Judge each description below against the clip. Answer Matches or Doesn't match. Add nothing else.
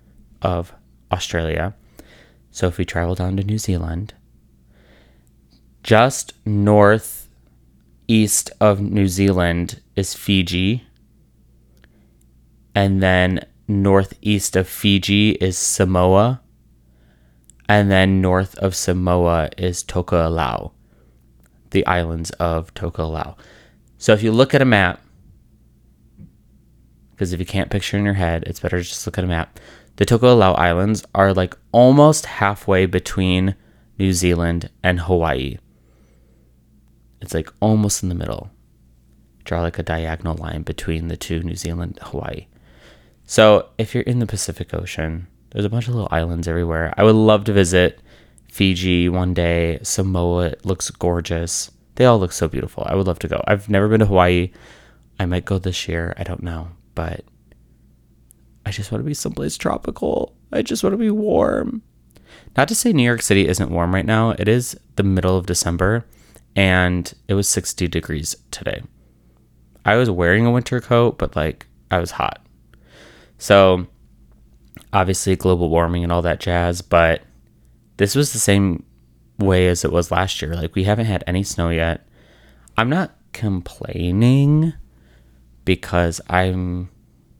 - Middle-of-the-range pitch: Doesn't match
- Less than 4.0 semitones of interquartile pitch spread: Matches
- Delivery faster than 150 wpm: Doesn't match